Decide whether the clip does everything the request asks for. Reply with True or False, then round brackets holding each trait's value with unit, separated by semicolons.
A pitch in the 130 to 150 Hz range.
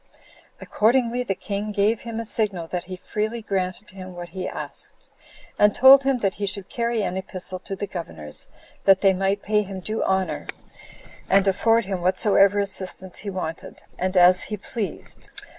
False (195 Hz)